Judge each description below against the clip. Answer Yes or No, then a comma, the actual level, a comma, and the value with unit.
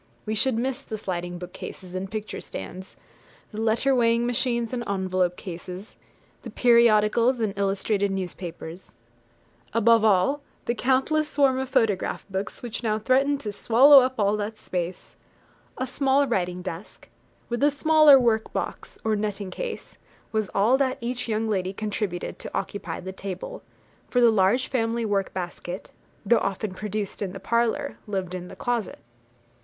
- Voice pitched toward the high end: Yes, high, 215 Hz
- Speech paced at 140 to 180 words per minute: Yes, average, 155 wpm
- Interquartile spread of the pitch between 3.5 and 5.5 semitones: Yes, average, 4.3 semitones